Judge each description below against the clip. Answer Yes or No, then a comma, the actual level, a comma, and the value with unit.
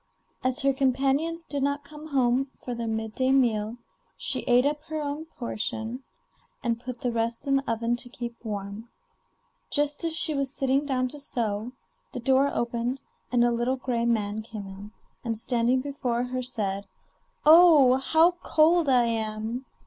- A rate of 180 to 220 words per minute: No, average, 170 wpm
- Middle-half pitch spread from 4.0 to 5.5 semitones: No, average, 3.2 semitones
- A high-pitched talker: Yes, very high, 250 Hz